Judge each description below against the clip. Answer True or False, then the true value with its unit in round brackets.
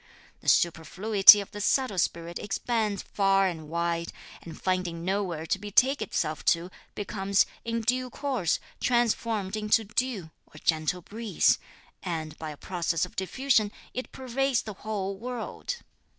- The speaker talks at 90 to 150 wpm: True (140 wpm)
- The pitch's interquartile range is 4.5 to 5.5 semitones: True (4.9 semitones)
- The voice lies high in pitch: True (200 Hz)